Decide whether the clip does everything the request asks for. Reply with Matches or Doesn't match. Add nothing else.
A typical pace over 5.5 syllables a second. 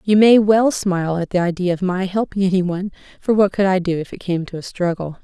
Matches